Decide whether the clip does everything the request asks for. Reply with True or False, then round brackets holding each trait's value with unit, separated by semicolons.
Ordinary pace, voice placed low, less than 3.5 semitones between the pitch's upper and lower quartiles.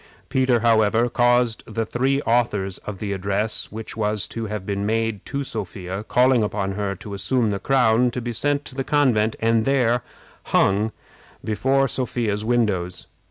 True (160 wpm; 115 Hz; 3.1 semitones)